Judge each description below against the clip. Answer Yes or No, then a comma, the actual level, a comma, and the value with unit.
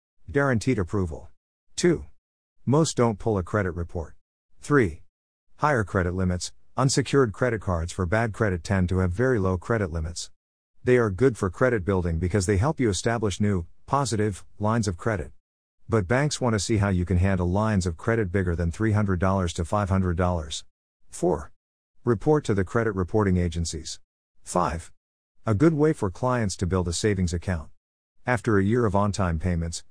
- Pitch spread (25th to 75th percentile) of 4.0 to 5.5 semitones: Yes, average, 4.6 semitones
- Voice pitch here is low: Yes, very low, 95 Hz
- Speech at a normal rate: Yes, average, 170 wpm